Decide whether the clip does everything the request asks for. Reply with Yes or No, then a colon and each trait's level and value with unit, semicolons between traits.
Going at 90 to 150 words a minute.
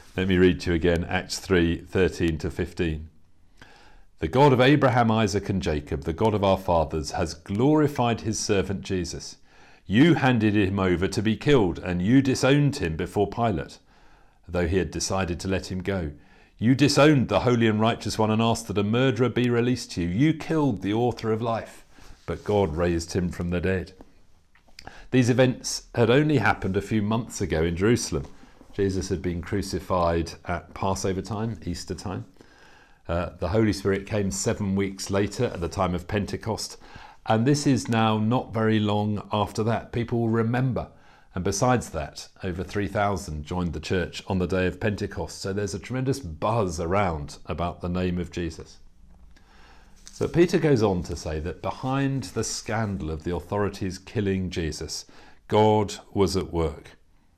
No: average, 175 wpm